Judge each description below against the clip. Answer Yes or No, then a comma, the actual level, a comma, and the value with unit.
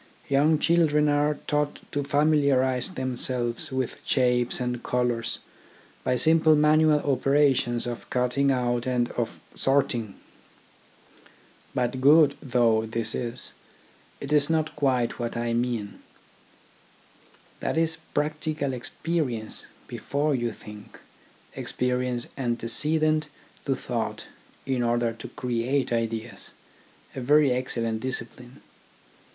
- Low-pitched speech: Yes, low, 130 Hz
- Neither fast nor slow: No, slow, 110 wpm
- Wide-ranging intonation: No, average, 3.6 semitones